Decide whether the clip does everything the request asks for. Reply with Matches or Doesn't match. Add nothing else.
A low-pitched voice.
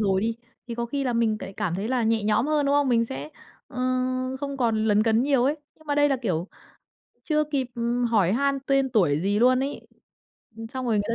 Doesn't match